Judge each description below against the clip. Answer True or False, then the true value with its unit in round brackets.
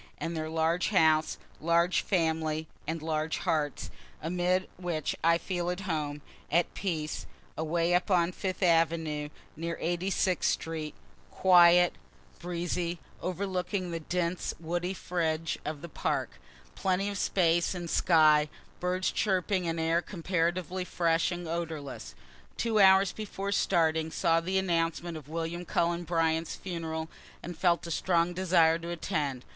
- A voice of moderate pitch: True (170 Hz)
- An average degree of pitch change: False (1.9 semitones)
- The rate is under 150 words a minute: True (140 wpm)